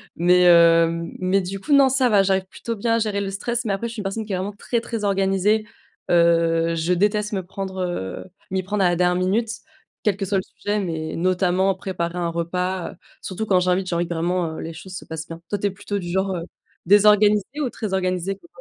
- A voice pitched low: No, high, 190 Hz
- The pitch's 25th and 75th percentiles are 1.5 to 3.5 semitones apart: Yes, average, 2.8 semitones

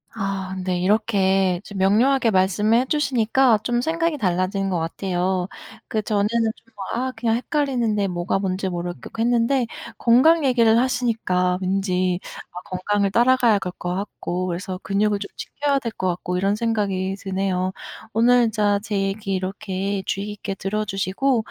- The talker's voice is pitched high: Yes, high, 200 Hz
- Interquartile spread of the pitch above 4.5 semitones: No, average, 3.7 semitones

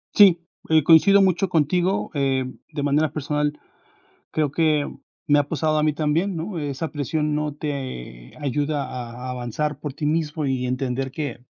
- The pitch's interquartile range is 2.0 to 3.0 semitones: Yes, average, 2.7 semitones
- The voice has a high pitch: No, medium, 150 Hz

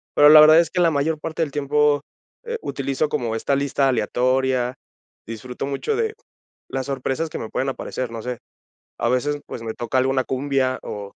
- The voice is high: No, low, 135 Hz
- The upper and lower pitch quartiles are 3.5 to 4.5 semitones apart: No, average, 2.8 semitones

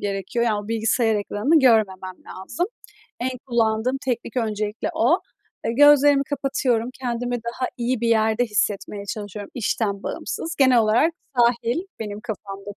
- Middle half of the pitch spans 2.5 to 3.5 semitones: Yes, average, 3.2 semitones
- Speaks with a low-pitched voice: No, high, 230 Hz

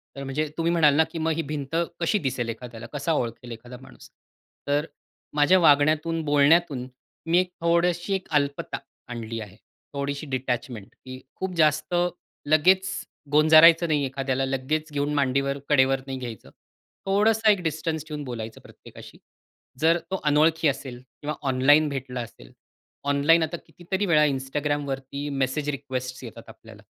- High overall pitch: No, medium, 145 Hz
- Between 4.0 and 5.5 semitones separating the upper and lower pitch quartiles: No, average, 3.4 semitones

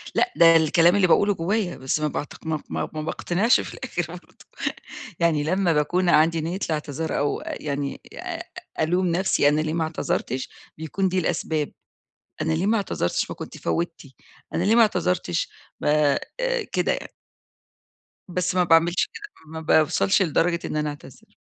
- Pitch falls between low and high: Yes, medium, 165 Hz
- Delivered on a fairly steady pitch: No, average, 3.0 semitones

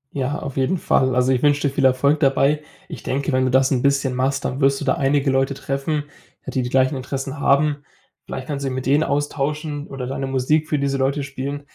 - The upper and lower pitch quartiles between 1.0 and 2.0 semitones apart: Yes, narrow, 1.6 semitones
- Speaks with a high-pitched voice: No, low, 135 Hz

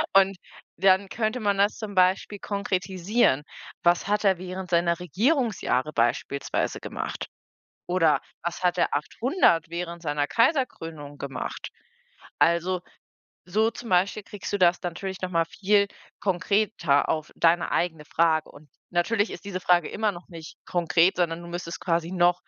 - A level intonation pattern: No, average, 3.2 semitones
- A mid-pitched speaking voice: Yes, medium, 180 Hz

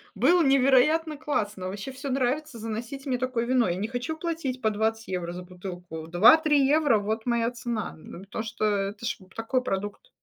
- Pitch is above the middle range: Yes, high, 235 Hz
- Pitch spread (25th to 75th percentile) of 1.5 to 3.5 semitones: No, average, 5.0 semitones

